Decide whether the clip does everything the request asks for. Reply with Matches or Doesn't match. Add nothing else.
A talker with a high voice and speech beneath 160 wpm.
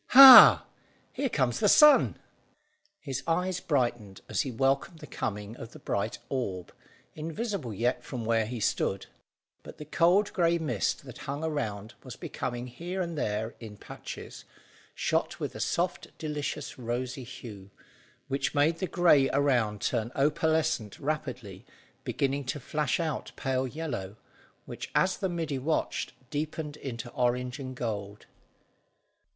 Doesn't match